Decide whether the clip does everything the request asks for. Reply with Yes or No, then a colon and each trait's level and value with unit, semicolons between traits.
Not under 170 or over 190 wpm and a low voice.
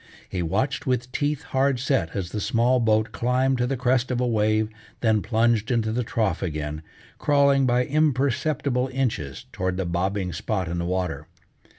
Yes: average, 175 wpm; low, 115 Hz